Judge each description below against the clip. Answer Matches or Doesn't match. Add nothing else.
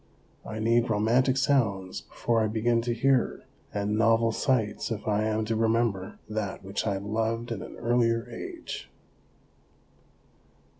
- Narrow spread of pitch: Matches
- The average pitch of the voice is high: Doesn't match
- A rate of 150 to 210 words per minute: Doesn't match